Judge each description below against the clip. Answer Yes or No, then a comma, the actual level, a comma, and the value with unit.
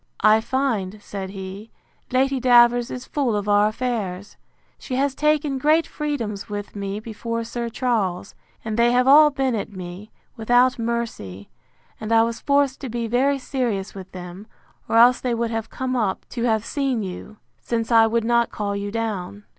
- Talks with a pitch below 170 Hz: No, high, 230 Hz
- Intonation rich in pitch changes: No, average, 3.6 semitones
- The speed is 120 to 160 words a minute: No, average, 180 wpm